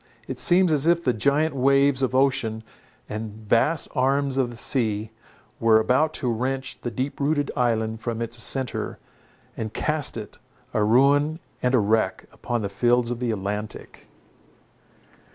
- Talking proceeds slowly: No, average, 155 wpm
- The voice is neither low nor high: No, low, 125 Hz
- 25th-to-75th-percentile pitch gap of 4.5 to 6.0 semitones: No, average, 3.8 semitones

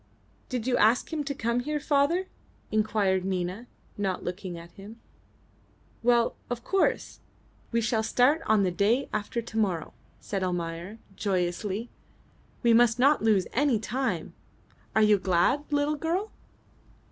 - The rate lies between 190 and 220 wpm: No, average, 140 wpm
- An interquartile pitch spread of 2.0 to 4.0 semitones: No, average, 4.9 semitones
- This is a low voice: No, high, 220 Hz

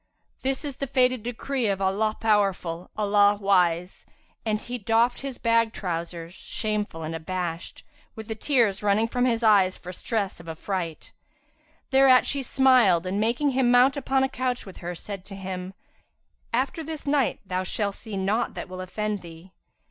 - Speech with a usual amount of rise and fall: Yes, average, 5.0 semitones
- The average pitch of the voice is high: Yes, high, 210 Hz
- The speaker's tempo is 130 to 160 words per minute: No, average, 175 wpm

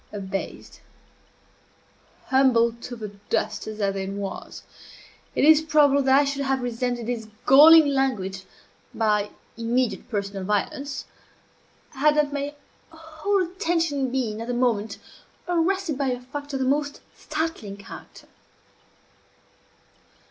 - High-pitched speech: Yes, very high, 265 Hz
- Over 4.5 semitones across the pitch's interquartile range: Yes, average, 5.0 semitones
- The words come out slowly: Yes, slow, 125 wpm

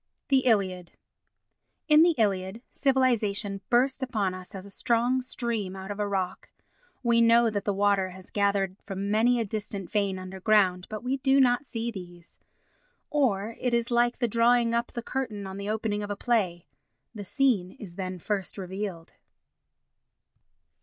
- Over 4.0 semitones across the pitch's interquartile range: No, average, 3.7 semitones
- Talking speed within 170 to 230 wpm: No, average, 160 wpm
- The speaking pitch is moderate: No, high, 210 Hz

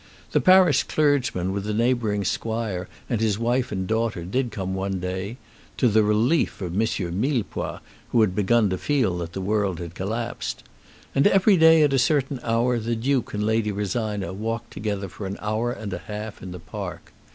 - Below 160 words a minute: No, average, 190 wpm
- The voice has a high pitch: No, low, 110 Hz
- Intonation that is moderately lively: Yes, average, 3.9 semitones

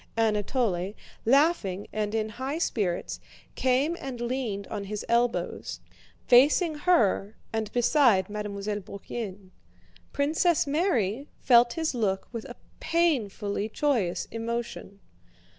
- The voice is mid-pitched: No, high, 230 Hz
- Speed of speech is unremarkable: No, slow, 110 wpm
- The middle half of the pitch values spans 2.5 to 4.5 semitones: No, average, 5.1 semitones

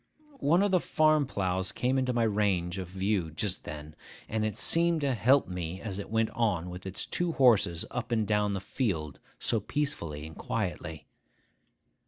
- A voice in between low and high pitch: No, low, 105 Hz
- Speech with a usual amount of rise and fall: No, wide, 6.0 semitones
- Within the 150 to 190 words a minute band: Yes, average, 180 wpm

